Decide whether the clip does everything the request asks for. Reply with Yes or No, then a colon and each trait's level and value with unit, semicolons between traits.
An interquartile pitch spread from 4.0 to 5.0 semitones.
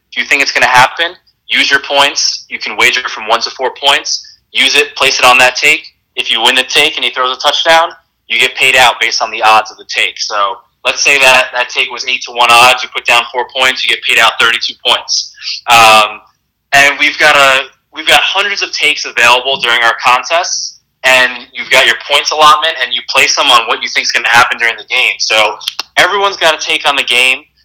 No: average, 3.6 semitones